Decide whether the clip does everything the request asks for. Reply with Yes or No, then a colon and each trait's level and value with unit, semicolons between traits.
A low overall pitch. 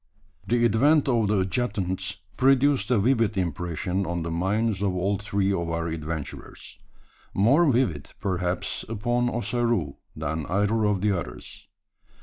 Yes: low, 100 Hz